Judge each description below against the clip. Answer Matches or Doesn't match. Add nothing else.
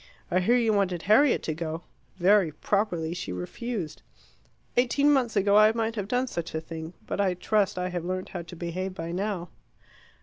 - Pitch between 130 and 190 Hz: Matches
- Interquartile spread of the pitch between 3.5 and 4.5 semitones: Matches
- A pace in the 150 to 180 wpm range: Doesn't match